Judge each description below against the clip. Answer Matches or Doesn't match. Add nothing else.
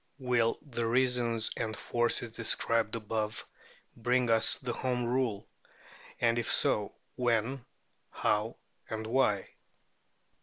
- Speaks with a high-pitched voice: Doesn't match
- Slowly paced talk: Matches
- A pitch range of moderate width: Doesn't match